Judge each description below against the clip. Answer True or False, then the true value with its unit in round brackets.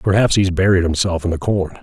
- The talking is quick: True (230 wpm)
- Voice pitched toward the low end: True (90 Hz)